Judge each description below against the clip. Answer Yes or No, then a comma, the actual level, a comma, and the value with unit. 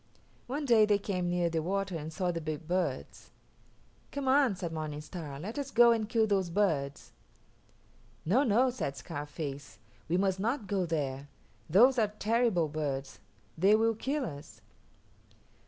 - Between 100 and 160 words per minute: Yes, average, 155 wpm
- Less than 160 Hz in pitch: No, medium, 185 Hz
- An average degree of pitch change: No, wide, 6.4 semitones